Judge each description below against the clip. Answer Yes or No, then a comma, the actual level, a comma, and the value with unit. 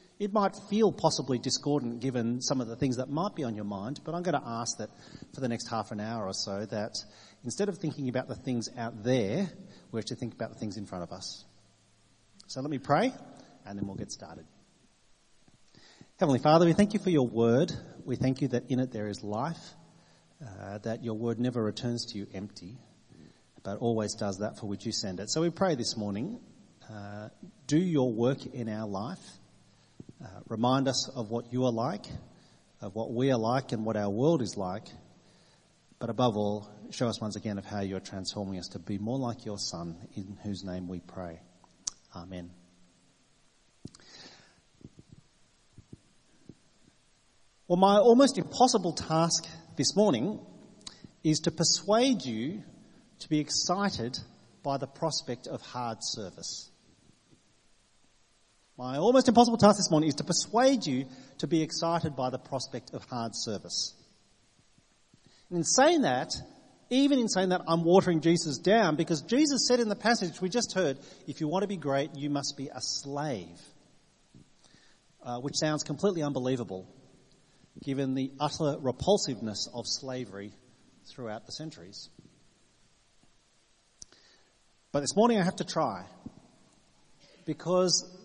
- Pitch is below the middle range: Yes, low, 130 Hz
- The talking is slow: No, average, 165 wpm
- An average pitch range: No, wide, 7.2 semitones